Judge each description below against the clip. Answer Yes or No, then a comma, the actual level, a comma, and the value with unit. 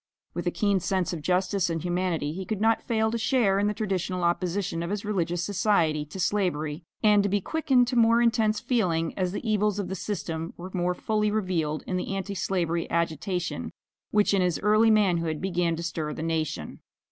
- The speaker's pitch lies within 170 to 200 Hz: Yes, medium, 185 Hz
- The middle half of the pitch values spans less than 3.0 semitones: No, average, 3.7 semitones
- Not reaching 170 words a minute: No, average, 200 wpm